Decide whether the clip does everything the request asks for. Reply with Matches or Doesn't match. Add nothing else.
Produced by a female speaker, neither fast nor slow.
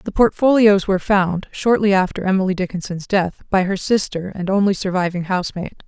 Matches